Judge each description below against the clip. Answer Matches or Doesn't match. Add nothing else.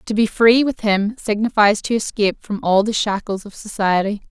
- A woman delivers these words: Matches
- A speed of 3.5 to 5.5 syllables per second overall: Matches